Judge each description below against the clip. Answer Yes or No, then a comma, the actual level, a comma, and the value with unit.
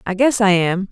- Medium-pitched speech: No, high, 200 Hz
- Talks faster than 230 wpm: Yes, fast, 265 wpm